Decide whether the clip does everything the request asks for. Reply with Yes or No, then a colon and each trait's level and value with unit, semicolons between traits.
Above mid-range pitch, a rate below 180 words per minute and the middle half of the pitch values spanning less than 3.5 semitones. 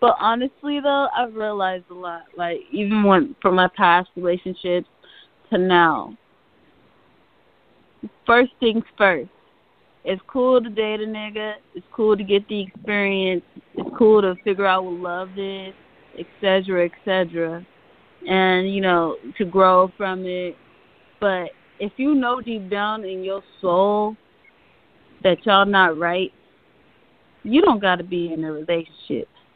Yes: high, 195 Hz; average, 140 wpm; average, 3.0 semitones